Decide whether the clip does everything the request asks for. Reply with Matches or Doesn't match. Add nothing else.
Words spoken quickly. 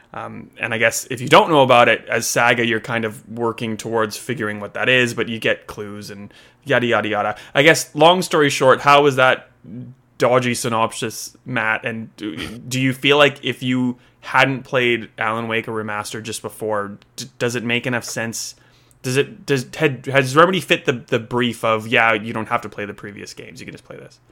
Matches